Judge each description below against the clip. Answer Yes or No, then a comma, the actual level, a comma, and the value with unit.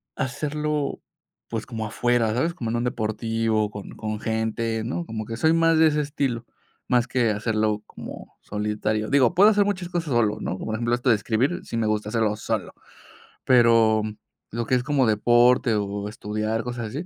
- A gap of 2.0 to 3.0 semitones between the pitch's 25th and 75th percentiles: No, average, 3.4 semitones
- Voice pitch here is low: Yes, low, 115 Hz